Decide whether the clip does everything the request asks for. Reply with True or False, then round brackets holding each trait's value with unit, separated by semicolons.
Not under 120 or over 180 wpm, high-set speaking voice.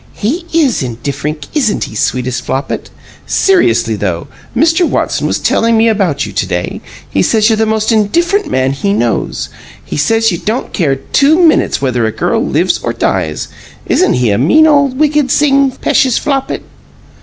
True (170 wpm; 215 Hz)